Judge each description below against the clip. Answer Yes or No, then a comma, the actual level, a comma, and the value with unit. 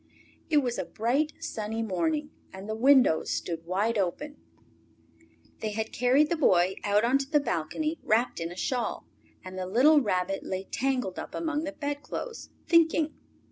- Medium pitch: No, high, 240 Hz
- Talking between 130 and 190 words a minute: Yes, average, 165 wpm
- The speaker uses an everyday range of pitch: No, wide, 7.3 semitones